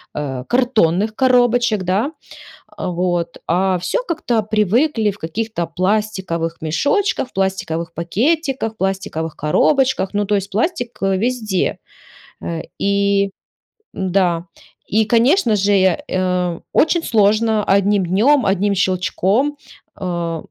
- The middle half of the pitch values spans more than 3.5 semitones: Yes, average, 4.1 semitones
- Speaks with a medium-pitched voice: No, high, 200 Hz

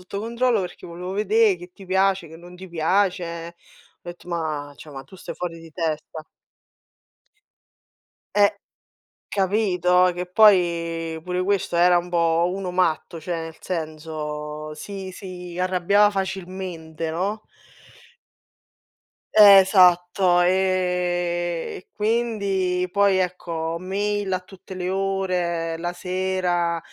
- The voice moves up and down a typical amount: No, narrow, 2.2 semitones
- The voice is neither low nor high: Yes, medium, 180 Hz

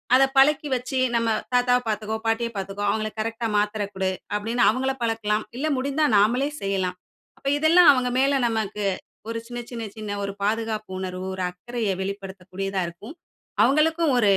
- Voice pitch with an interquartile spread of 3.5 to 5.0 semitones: Yes, average, 4.1 semitones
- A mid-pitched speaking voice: No, high, 225 Hz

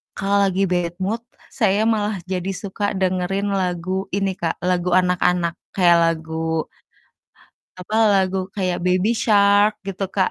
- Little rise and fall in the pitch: Yes, narrow, 2.0 semitones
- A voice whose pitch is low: No, medium, 185 Hz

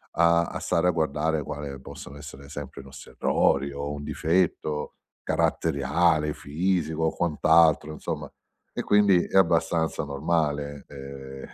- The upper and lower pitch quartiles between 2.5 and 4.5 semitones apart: Yes, average, 2.8 semitones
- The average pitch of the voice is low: Yes, very low, 75 Hz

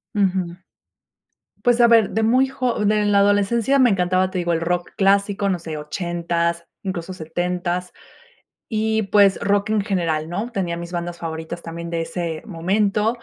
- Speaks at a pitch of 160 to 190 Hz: Yes, medium, 185 Hz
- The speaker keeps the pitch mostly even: No, average, 3.5 semitones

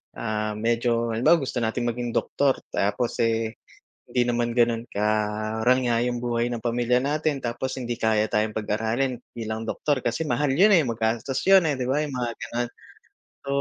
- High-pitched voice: No, low, 120 Hz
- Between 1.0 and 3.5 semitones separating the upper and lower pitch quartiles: Yes, narrow, 2.5 semitones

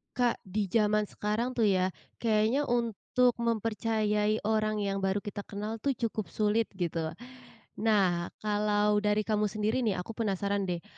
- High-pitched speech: Yes, high, 210 Hz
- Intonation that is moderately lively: No, narrow, 1.8 semitones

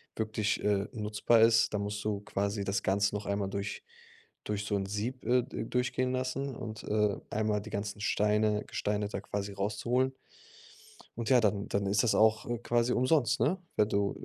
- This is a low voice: Yes, low, 105 Hz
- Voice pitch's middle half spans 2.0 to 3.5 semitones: Yes, narrow, 2.6 semitones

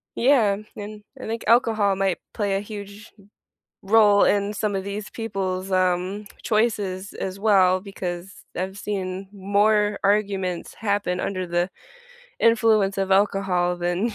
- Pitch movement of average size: No, narrow, 2.0 semitones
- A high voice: Yes, high, 200 Hz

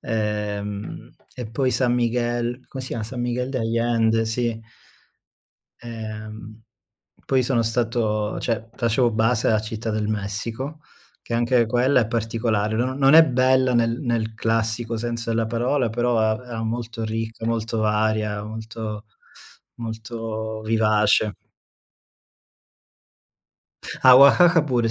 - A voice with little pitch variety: Yes, narrow, 1.8 semitones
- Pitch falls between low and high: No, low, 115 Hz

